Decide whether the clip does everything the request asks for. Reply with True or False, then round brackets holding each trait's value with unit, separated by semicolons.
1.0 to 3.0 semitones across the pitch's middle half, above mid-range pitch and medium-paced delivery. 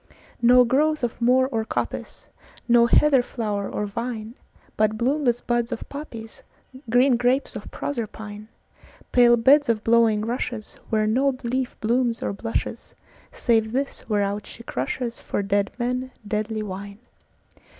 False (2.7 semitones; 235 Hz; 115 wpm)